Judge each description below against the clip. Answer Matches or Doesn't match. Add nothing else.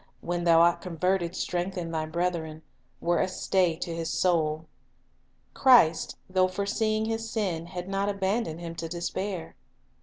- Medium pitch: Matches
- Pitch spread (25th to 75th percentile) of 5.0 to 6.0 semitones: Doesn't match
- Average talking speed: Matches